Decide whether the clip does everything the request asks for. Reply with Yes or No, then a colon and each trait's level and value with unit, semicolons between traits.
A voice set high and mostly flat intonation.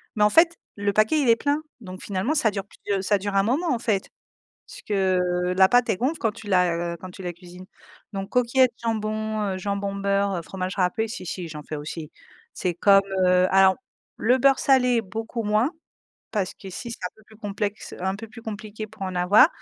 No: high, 205 Hz; average, 3.4 semitones